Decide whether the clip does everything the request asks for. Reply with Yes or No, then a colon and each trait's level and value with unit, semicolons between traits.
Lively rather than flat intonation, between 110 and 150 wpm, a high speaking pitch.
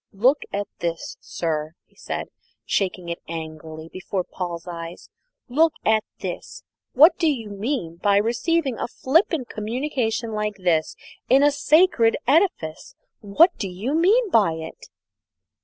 Yes: wide, 8.6 semitones; average, 140 wpm; high, 215 Hz